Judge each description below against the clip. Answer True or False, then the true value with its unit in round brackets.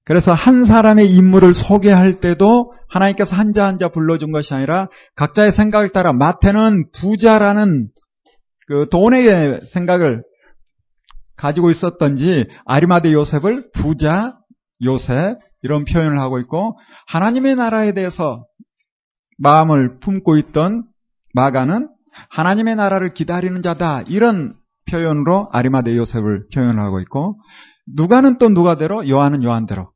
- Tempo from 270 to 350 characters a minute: True (295 characters per minute)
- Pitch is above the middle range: False (180 Hz)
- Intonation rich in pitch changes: True (6.1 semitones)